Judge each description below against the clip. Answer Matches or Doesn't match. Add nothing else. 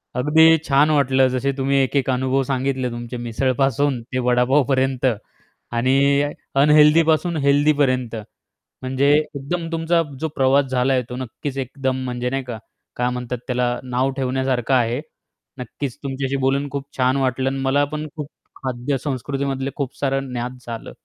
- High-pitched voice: Doesn't match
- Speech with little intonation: Matches